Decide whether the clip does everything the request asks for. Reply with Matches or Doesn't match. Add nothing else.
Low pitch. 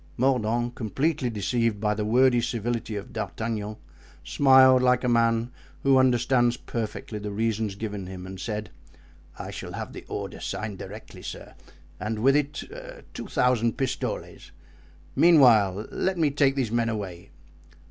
Matches